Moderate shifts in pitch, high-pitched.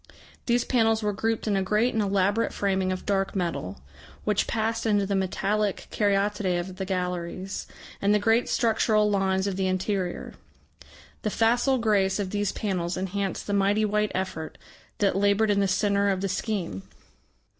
No: narrow, 1.9 semitones; high, 200 Hz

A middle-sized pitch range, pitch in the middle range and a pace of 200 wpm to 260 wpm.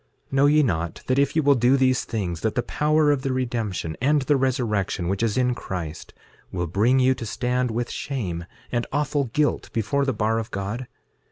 No: average, 4.4 semitones; low, 125 Hz; fast, 205 wpm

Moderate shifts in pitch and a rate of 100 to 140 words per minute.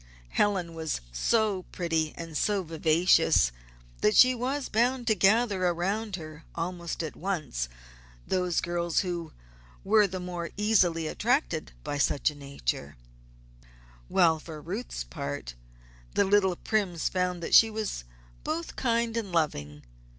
Yes: average, 4.7 semitones; slow, 135 wpm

